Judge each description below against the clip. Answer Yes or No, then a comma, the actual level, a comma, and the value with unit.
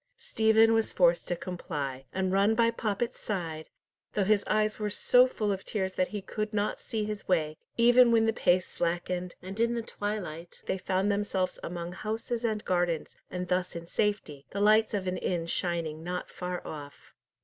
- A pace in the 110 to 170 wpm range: No, average, 185 wpm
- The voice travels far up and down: No, average, 3.5 semitones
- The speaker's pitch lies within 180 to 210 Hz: Yes, high, 190 Hz